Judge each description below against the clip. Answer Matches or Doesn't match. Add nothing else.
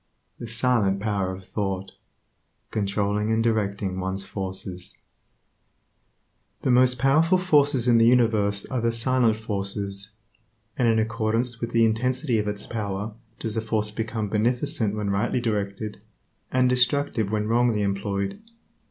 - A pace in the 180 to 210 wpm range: Doesn't match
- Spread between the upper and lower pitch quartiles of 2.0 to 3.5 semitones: Matches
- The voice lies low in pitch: Matches